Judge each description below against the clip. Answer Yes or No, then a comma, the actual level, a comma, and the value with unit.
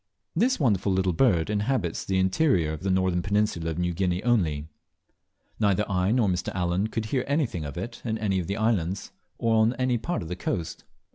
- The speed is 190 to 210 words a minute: Yes, average, 200 wpm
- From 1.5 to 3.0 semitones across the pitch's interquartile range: No, average, 4.2 semitones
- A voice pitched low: Yes, very low, 95 Hz